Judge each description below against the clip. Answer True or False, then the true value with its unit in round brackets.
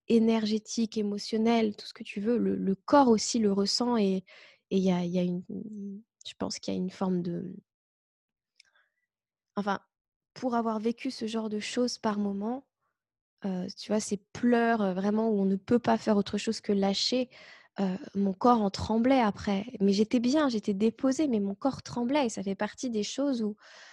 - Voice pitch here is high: True (215 Hz)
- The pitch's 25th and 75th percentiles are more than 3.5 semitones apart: False (2.8 semitones)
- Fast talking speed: False (190 wpm)